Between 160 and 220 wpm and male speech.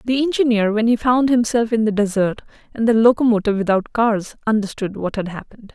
No: average, 190 wpm; female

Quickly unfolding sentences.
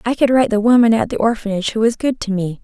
Yes: fast, 295 wpm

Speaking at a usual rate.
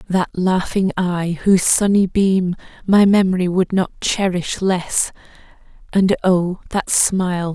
No: slow, 125 wpm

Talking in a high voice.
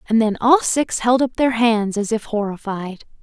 Yes: high, 230 Hz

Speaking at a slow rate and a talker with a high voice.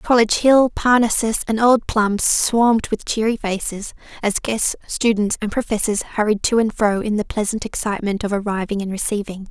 No: average, 170 wpm; high, 215 Hz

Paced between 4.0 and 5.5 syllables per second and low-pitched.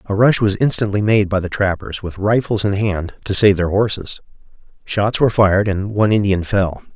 Yes: 5.3 syllables/s; low, 100 Hz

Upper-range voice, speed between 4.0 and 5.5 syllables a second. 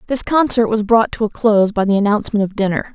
No: high, 215 Hz; 6.5 syllables/s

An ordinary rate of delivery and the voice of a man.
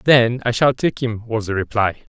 No: fast, 225 wpm; male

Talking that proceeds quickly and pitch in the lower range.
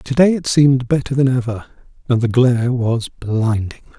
No: average, 180 wpm; low, 125 Hz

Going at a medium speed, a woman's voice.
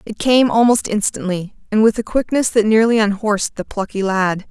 Yes: average, 185 wpm; female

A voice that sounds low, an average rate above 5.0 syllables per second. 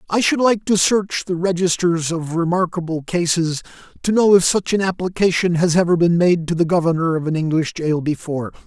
No: medium, 175 Hz; 5.4 syllables/s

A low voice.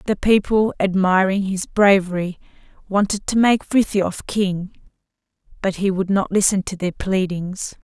No: high, 195 Hz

